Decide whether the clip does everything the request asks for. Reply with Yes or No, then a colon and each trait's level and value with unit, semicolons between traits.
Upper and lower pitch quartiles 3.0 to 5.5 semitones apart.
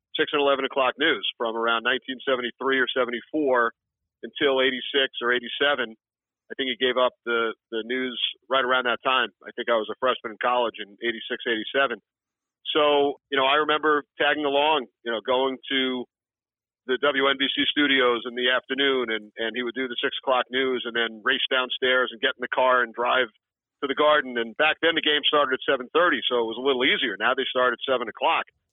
No: narrow, 2.5 semitones